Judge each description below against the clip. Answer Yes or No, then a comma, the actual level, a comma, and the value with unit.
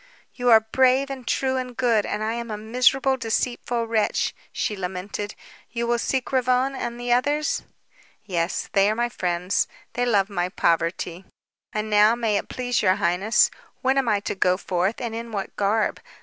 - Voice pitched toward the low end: No, high, 225 Hz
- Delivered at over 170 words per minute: Yes, average, 180 wpm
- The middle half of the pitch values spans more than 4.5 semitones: No, average, 3.7 semitones